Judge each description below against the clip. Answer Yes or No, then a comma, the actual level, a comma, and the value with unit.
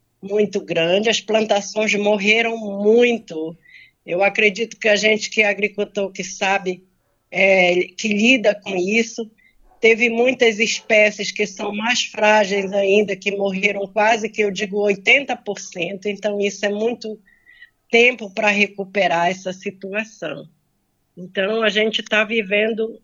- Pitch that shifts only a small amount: Yes, narrow, 2.0 semitones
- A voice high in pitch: Yes, high, 210 Hz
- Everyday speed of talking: Yes, average, 130 wpm